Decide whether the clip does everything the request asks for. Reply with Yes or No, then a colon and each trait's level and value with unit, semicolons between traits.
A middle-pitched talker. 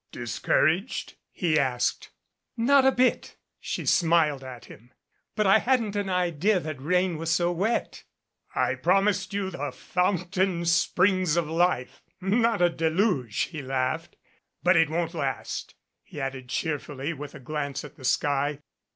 Yes: medium, 170 Hz